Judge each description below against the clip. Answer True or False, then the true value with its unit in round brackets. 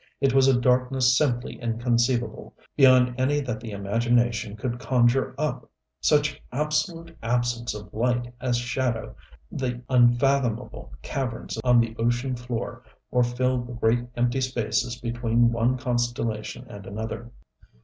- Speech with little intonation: True (1.6 semitones)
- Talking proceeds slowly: True (130 wpm)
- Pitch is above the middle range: False (120 Hz)